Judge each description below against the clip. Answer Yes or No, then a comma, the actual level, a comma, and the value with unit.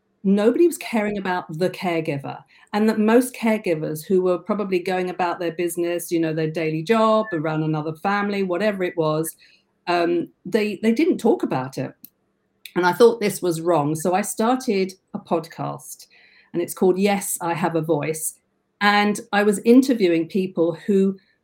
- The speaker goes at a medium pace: Yes, average, 170 wpm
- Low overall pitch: No, medium, 185 Hz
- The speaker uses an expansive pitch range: No, average, 3.6 semitones